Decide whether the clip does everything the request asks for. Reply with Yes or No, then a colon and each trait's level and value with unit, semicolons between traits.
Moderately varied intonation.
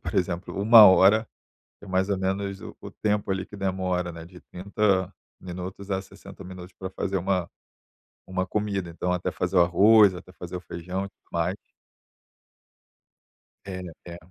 No: narrow, 1.6 semitones